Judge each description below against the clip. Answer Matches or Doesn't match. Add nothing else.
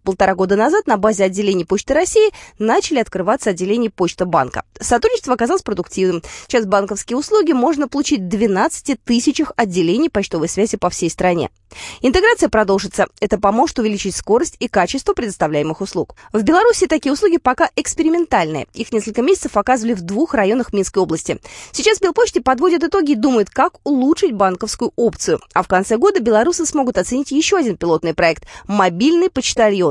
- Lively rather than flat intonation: Matches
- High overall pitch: Matches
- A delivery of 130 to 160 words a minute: Matches